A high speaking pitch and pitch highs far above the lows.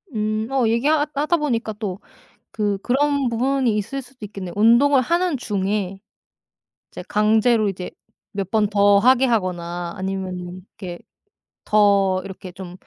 No: high, 210 Hz; average, 4.5 semitones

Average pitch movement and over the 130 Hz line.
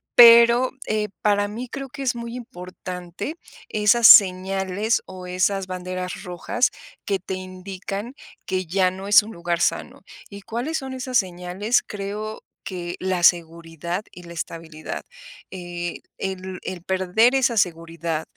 Yes: average, 3.4 semitones; high, 190 Hz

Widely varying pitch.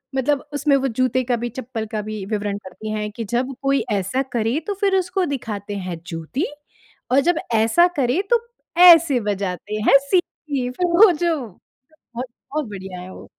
Yes: wide, 5.7 semitones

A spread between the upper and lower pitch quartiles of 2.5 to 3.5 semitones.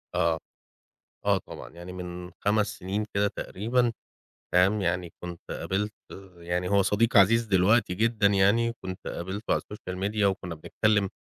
Yes: average, 2.9 semitones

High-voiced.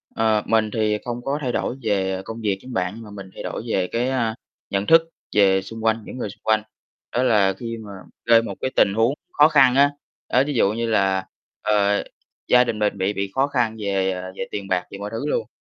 No: low, 110 Hz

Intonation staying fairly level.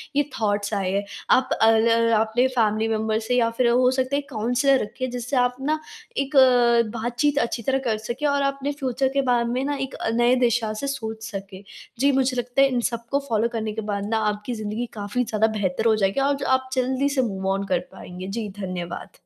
No: average, 3.3 semitones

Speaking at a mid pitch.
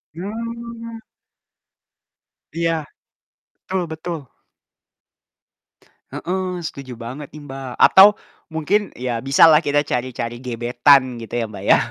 Yes: medium, 150 Hz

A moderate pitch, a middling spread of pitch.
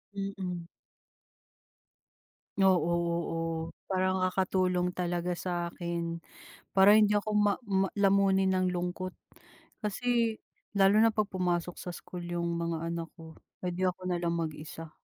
No: medium, 180 Hz; narrow, 2.1 semitones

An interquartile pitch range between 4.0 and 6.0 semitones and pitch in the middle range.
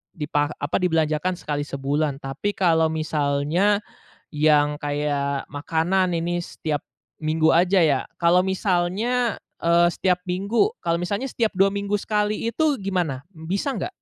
Yes: average, 4.6 semitones; medium, 170 Hz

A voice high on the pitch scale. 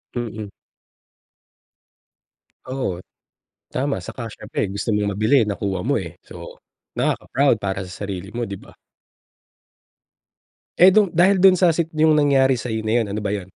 No: low, 115 Hz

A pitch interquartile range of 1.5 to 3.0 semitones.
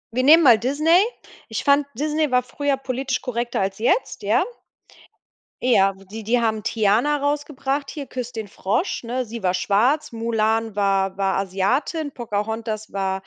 No: average, 5.1 semitones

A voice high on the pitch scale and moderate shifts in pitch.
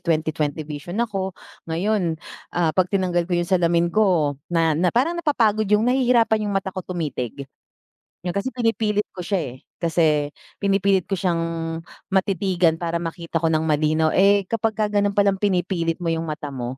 No: medium, 175 Hz; average, 3.7 semitones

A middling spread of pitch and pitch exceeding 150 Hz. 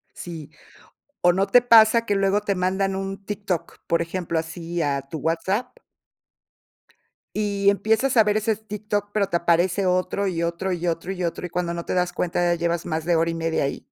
Yes: average, 3.1 semitones; medium, 185 Hz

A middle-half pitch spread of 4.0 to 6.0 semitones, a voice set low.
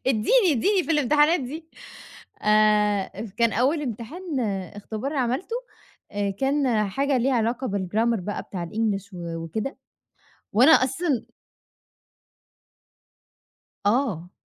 No: average, 5.2 semitones; high, 235 Hz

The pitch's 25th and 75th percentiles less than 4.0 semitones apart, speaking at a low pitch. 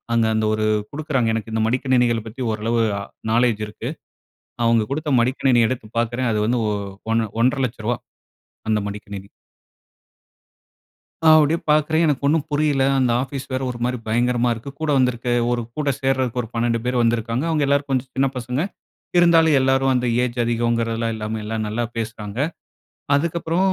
Yes: average, 3.1 semitones; low, 125 Hz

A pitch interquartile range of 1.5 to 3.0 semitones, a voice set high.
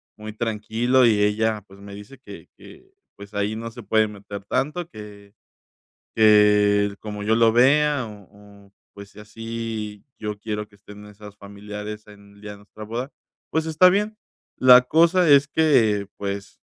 No: average, 2.7 semitones; low, 105 Hz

